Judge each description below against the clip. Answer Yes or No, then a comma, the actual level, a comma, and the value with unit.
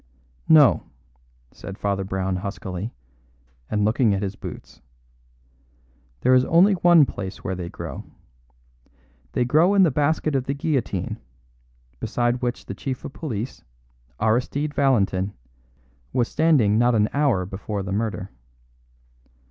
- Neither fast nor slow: No, slow, 130 wpm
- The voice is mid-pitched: No, low, 120 Hz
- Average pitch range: No, wide, 6.2 semitones